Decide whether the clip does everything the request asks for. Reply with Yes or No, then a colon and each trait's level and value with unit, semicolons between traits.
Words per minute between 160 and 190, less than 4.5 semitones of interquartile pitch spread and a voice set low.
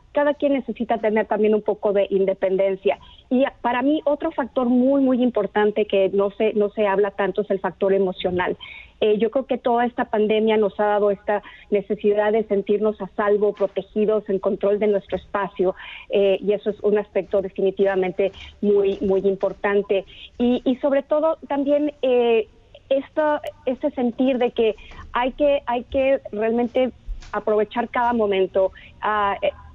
No: average, 165 wpm; average, 3.9 semitones; high, 215 Hz